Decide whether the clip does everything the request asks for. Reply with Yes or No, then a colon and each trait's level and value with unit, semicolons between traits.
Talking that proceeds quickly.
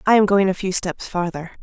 Yes: fast, 260 wpm